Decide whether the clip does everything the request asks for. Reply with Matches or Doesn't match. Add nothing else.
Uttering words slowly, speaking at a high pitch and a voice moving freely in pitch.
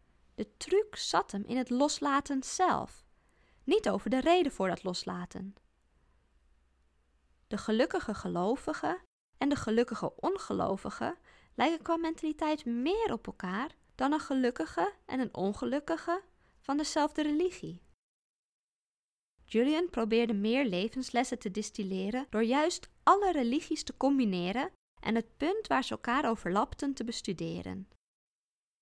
Matches